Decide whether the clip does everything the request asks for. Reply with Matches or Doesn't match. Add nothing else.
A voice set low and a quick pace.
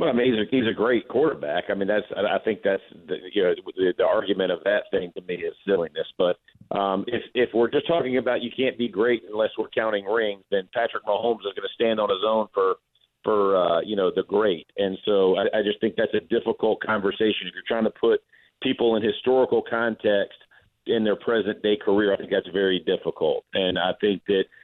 Matches